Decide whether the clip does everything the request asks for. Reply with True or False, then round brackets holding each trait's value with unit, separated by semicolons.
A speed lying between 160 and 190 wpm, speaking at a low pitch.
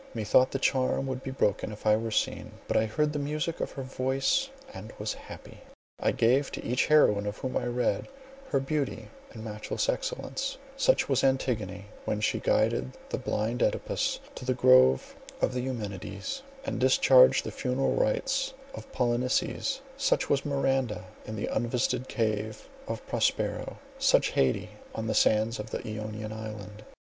True (165 wpm; 125 Hz)